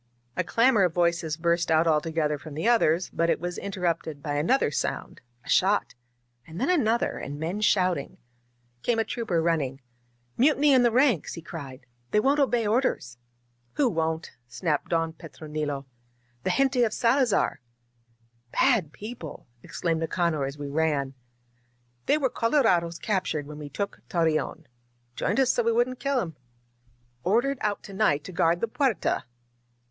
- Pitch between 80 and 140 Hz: No, medium, 170 Hz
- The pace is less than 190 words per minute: Yes, average, 165 wpm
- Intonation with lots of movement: Yes, wide, 7.1 semitones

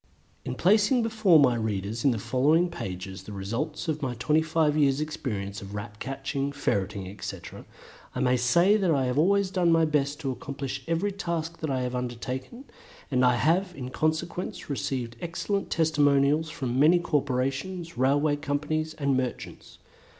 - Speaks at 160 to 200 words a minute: Yes, average, 165 wpm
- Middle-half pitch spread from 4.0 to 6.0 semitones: Yes, average, 4.6 semitones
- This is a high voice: No, medium, 145 Hz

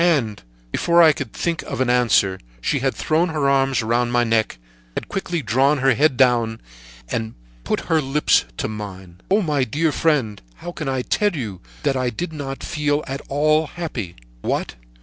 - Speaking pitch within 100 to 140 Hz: Yes, low, 135 Hz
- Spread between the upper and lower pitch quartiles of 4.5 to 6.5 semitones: Yes, average, 5.2 semitones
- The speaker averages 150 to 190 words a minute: Yes, average, 180 wpm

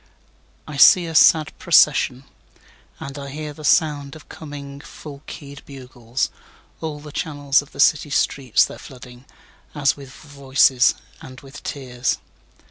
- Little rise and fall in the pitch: Yes, narrow, 1.9 semitones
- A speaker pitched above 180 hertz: No, medium, 140 Hz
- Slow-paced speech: Yes, slow, 125 wpm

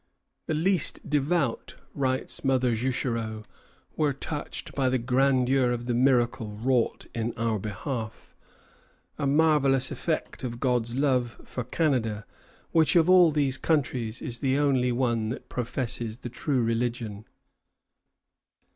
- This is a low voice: Yes, low, 125 Hz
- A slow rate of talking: Yes, slow, 130 wpm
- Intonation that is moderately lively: Yes, average, 3.0 semitones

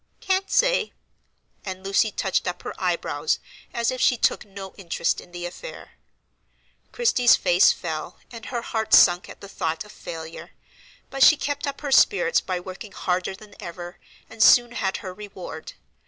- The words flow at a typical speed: Yes, average, 170 wpm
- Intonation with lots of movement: Yes, wide, 5.8 semitones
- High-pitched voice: Yes, high, 200 Hz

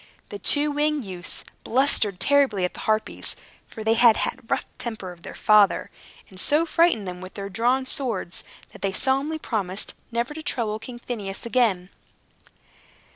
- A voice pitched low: No, high, 225 Hz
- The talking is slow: No, average, 165 wpm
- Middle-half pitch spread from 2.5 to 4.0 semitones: No, wide, 5.5 semitones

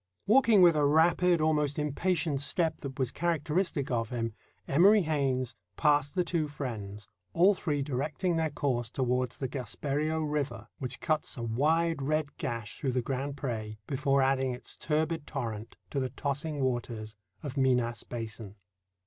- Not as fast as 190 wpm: Yes, average, 155 wpm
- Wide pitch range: No, average, 3.8 semitones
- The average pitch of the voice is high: No, medium, 140 Hz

